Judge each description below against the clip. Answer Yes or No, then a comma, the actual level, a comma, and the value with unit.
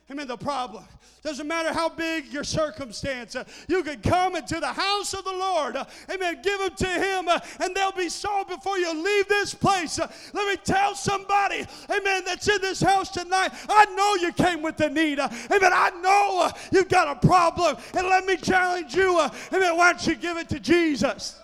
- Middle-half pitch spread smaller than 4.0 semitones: Yes, average, 3.3 semitones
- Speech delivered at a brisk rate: Yes, fast, 215 wpm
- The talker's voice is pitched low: No, very high, 350 Hz